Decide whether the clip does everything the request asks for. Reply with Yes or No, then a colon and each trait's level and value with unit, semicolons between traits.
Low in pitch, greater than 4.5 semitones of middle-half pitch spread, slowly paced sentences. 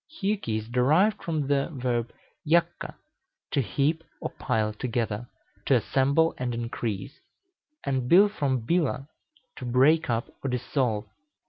Yes: low, 130 Hz; average, 4.9 semitones; slow, 130 wpm